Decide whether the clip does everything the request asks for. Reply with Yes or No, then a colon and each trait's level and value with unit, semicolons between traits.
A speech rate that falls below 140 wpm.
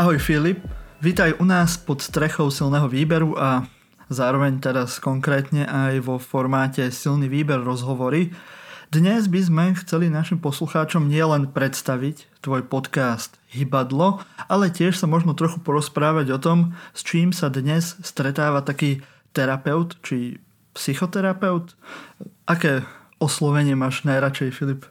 Yes: average, 125 wpm